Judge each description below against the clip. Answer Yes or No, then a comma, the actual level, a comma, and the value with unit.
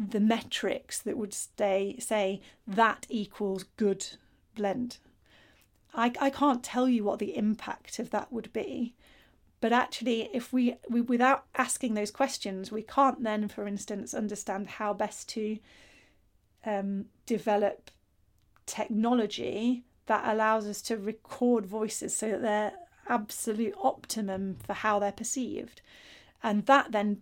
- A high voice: Yes, high, 220 Hz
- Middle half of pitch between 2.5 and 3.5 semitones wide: Yes, average, 2.8 semitones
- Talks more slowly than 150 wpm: Yes, slow, 135 wpm